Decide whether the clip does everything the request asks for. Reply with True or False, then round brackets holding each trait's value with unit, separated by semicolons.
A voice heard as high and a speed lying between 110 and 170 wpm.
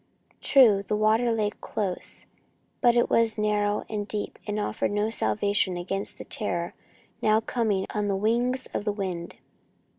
True (210 Hz; 155 wpm)